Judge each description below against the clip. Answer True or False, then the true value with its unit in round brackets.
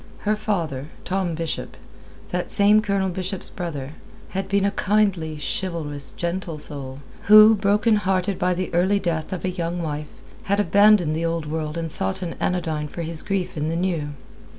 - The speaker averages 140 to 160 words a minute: False (175 wpm)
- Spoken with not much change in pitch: False (3.9 semitones)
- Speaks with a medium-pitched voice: True (175 Hz)